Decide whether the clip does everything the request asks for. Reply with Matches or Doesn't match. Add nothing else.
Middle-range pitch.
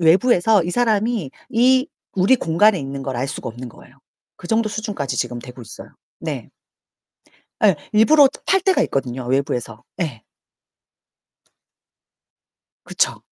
Matches